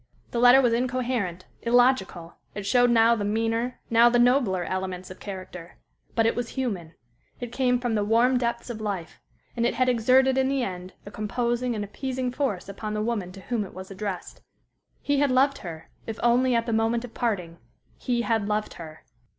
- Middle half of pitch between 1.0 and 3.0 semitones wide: No, average, 3.8 semitones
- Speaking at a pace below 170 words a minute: No, average, 195 wpm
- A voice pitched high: Yes, high, 230 Hz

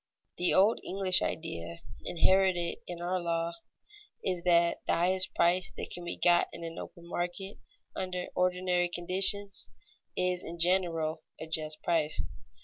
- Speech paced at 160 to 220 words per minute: No, average, 140 wpm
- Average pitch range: No, narrow, 1.5 semitones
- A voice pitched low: No, medium, 175 Hz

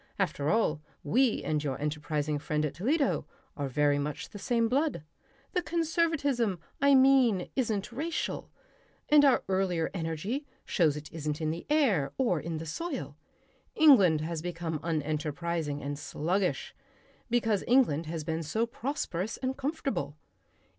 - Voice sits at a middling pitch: Yes, medium, 175 Hz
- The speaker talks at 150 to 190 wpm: No, average, 140 wpm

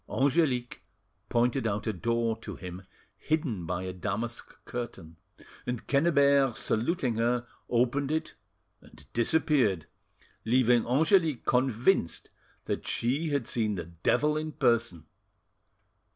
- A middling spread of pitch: Yes, average, 4.3 semitones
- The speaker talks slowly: Yes, slow, 115 wpm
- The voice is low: Yes, low, 120 Hz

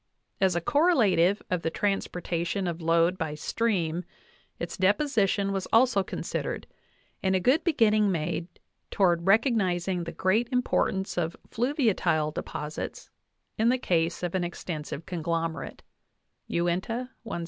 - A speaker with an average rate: No, slow, 130 wpm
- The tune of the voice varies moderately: Yes, average, 4.5 semitones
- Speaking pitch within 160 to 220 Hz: Yes, medium, 185 Hz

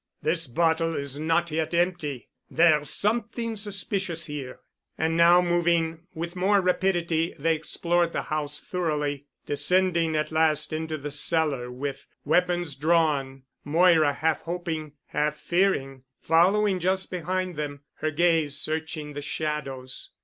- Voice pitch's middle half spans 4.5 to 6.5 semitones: No, average, 2.8 semitones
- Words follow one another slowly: Yes, slow, 130 wpm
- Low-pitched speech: No, medium, 160 Hz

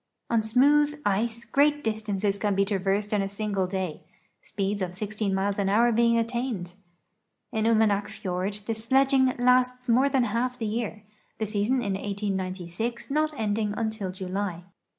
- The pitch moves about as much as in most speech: Yes, average, 3.1 semitones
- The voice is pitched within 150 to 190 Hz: No, high, 215 Hz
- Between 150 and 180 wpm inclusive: Yes, average, 155 wpm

